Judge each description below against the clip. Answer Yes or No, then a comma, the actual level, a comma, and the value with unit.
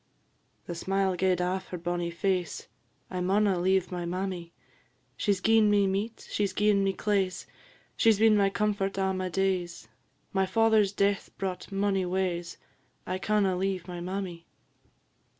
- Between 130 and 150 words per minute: No, average, 160 wpm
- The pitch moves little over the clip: Yes, narrow, 1.8 semitones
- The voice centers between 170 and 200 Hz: Yes, high, 190 Hz